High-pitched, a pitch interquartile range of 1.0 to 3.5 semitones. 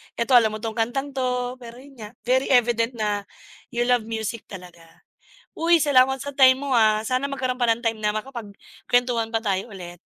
Yes: high, 240 Hz; average, 2.9 semitones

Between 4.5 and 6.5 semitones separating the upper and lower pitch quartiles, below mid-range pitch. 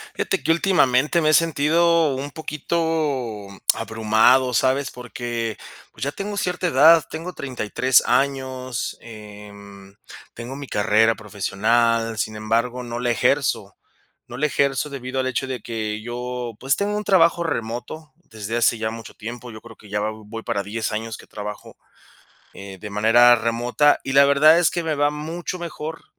Yes: average, 4.9 semitones; low, 125 Hz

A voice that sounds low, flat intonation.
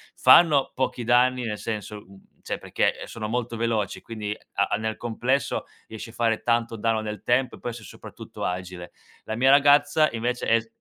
Yes: low, 115 Hz; narrow, 2.3 semitones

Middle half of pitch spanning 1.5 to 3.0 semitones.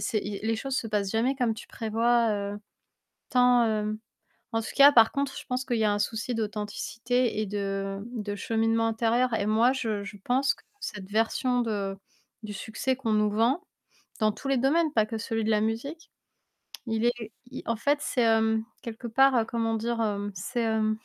Yes: narrow, 2.5 semitones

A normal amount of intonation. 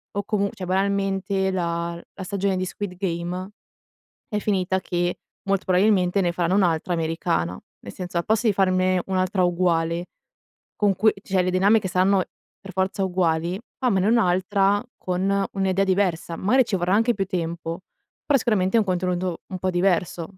No: narrow, 1.9 semitones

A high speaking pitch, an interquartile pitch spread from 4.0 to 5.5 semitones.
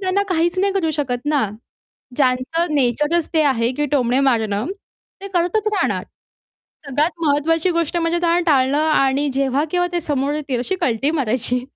Yes: very high, 295 Hz; average, 4.7 semitones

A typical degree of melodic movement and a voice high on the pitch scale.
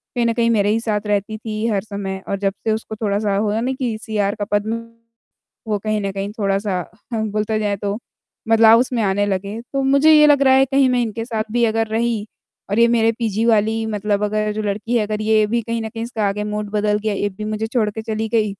No: narrow, 1.8 semitones; high, 215 Hz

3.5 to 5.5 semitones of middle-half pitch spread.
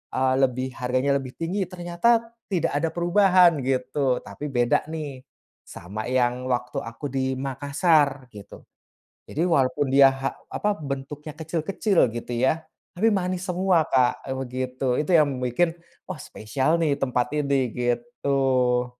Yes: average, 4.5 semitones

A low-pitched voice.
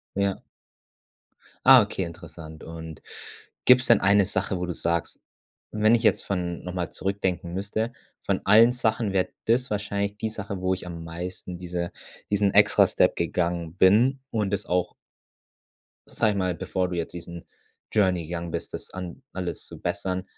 Yes: very low, 95 Hz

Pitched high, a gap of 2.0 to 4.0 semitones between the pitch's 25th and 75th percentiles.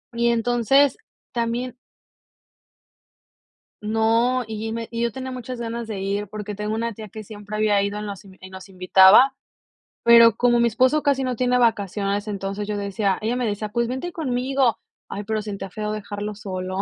Yes: high, 220 Hz; average, 2.8 semitones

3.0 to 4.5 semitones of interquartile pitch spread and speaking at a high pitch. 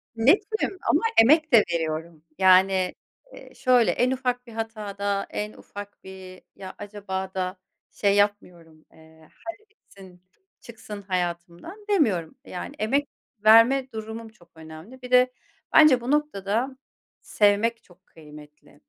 No: wide, 5.4 semitones; high, 205 Hz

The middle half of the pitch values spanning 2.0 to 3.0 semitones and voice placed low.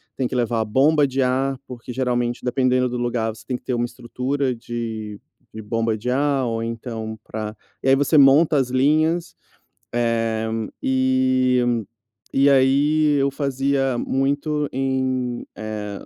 Yes: narrow, 2.6 semitones; low, 125 Hz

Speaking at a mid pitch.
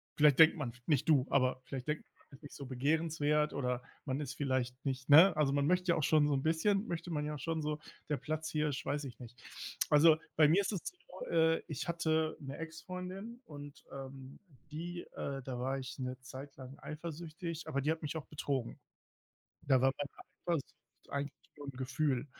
Yes: medium, 150 Hz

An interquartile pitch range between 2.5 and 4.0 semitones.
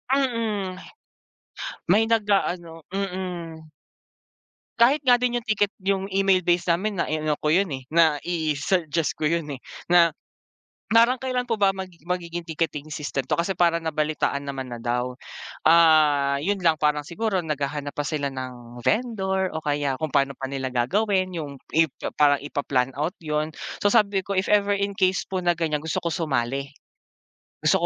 No: average, 4.8 semitones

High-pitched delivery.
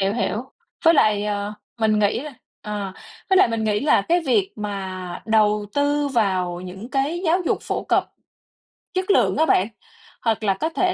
Yes: high, 215 Hz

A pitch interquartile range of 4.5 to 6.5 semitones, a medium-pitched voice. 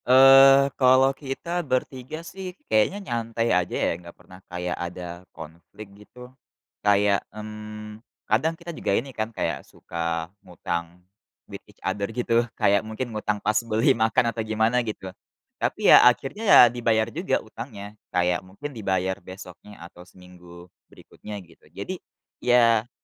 No: average, 5.2 semitones; low, 110 Hz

